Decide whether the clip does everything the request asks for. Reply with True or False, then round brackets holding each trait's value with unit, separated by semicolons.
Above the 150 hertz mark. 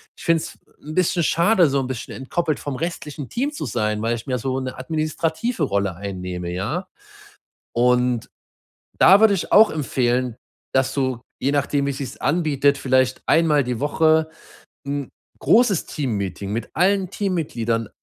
False (140 Hz)